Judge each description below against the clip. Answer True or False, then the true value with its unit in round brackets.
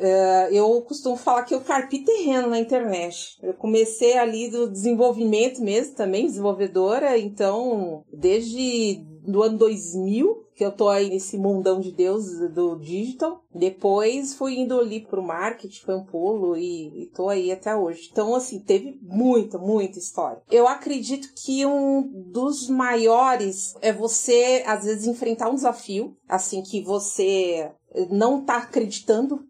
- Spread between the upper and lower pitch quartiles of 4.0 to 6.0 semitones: True (4.6 semitones)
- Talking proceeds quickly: False (150 wpm)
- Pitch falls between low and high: False (225 Hz)